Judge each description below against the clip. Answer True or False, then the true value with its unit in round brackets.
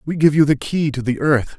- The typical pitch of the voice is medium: True (145 Hz)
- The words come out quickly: True (305 wpm)